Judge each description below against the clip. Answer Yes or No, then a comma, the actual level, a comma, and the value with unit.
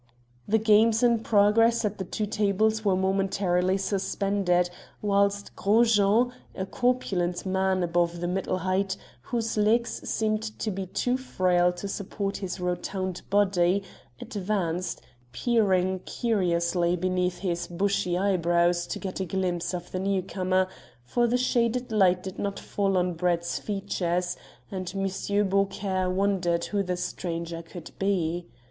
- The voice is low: No, high, 190 Hz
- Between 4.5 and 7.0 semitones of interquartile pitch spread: No, narrow, 2.5 semitones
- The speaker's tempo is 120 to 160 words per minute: Yes, average, 140 wpm